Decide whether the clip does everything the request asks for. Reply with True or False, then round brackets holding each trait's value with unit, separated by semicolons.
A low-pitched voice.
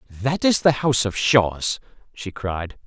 True (115 Hz)